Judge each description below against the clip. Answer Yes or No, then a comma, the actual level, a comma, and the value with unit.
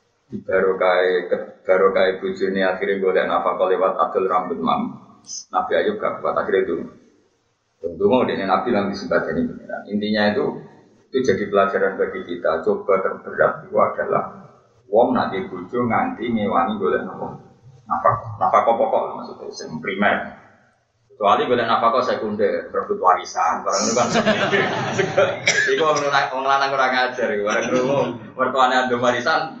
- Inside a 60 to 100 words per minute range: No, average, 145 wpm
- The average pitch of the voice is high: No, low, 130 Hz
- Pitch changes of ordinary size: No, wide, 8.8 semitones